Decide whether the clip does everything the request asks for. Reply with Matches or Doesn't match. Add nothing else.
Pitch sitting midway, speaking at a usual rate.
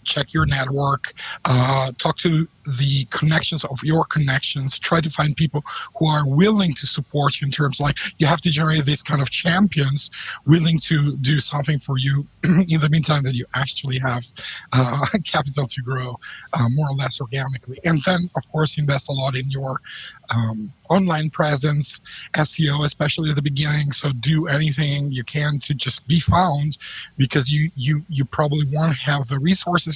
Matches